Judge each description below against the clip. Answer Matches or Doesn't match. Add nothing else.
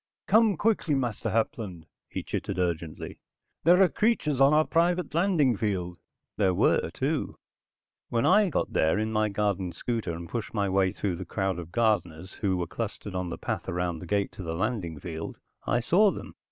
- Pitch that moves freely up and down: Matches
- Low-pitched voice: Matches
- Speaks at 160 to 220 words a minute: Matches